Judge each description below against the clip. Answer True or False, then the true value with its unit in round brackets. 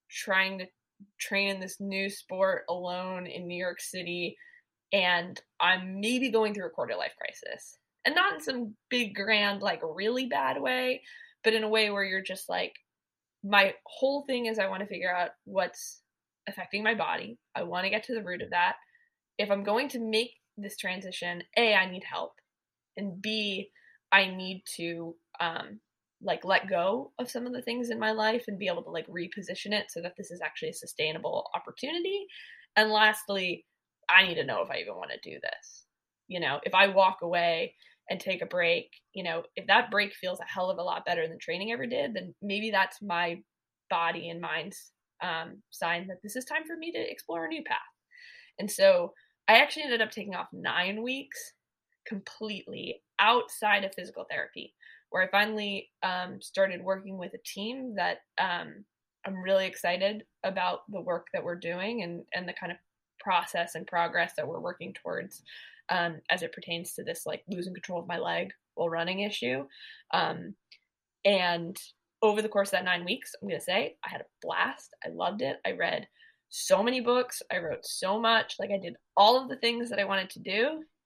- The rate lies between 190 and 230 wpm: True (195 wpm)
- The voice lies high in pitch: True (200 Hz)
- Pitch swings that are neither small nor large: True (4.5 semitones)